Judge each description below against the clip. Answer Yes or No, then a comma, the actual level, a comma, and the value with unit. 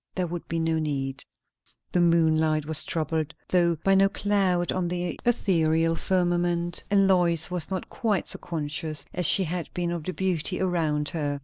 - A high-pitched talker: No, medium, 170 Hz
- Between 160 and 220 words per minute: Yes, average, 175 wpm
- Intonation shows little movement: Yes, narrow, 2.3 semitones